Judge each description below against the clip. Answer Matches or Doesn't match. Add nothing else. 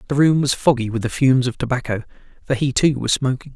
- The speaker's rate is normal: Doesn't match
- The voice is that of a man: Matches